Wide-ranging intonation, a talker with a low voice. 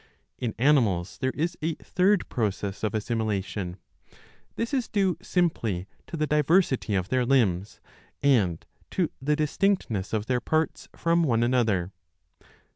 Yes: wide, 7.7 semitones; low, 125 Hz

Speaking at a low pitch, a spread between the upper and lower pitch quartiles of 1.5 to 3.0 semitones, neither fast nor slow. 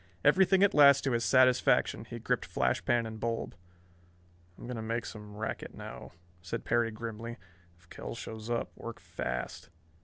Yes: low, 115 Hz; narrow, 2.4 semitones; average, 165 wpm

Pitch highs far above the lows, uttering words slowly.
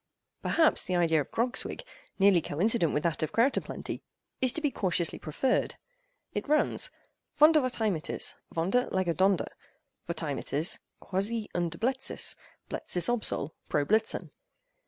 Yes: wide, 7.2 semitones; slow, 90 wpm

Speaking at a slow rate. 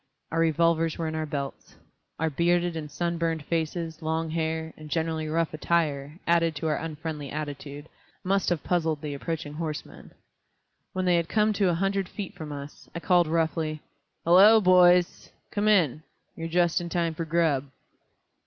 No: average, 170 wpm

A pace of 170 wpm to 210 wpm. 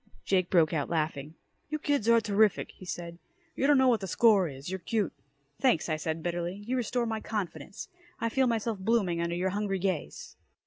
Yes: average, 195 wpm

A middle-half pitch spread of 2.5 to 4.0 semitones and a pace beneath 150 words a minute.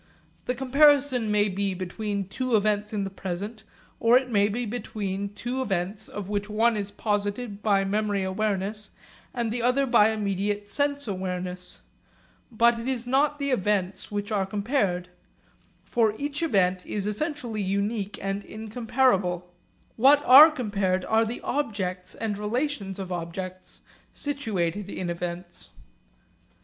Yes: average, 3.7 semitones; average, 140 wpm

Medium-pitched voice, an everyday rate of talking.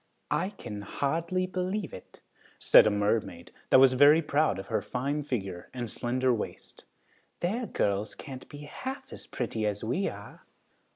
No: low, 130 Hz; average, 160 wpm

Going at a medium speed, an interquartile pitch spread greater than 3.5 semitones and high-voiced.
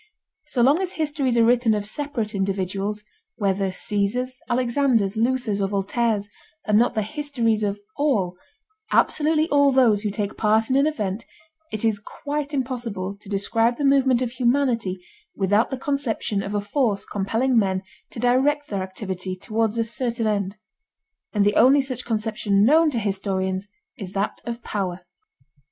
Yes: average, 160 wpm; average, 4.3 semitones; high, 225 Hz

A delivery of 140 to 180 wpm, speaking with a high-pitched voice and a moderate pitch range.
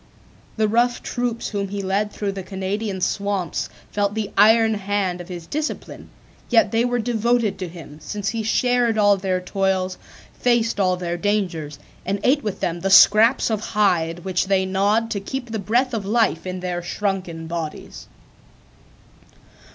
Yes: average, 165 wpm; high, 200 Hz; average, 3.3 semitones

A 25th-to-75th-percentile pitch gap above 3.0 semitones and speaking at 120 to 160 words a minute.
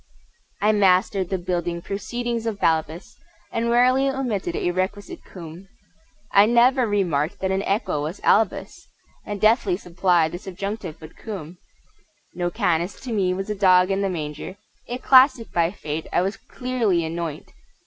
Yes: average, 4.0 semitones; average, 155 wpm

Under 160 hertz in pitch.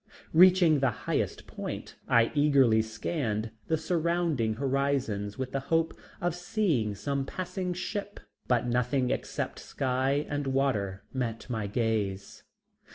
Yes: low, 135 Hz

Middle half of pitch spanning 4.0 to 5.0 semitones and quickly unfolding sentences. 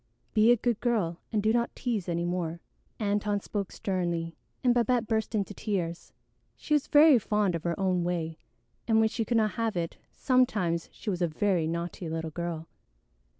No: average, 4.7 semitones; average, 185 wpm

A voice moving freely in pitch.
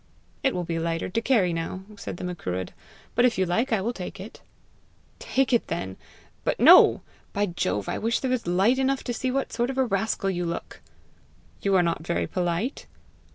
Yes: wide, 5.7 semitones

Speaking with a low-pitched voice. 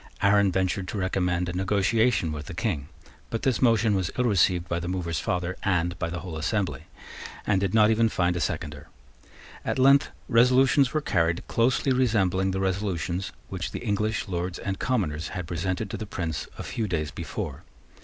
Yes: very low, 95 Hz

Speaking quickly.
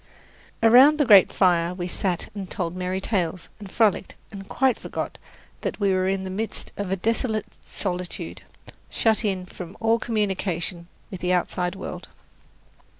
No: average, 155 wpm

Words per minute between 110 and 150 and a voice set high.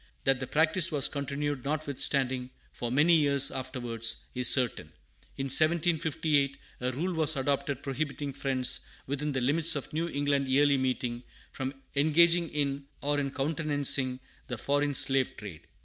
No: average, 140 wpm; medium, 140 Hz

